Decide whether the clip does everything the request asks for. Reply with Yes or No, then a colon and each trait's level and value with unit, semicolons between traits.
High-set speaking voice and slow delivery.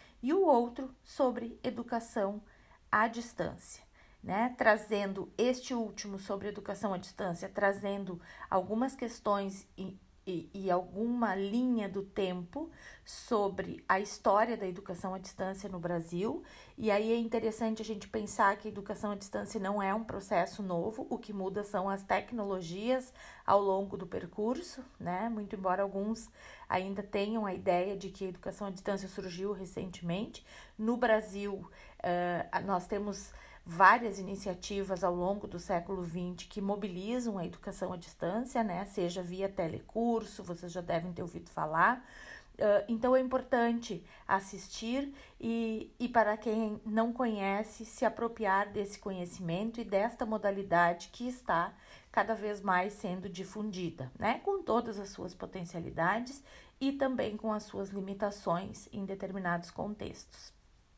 No: high, 200 Hz; average, 145 wpm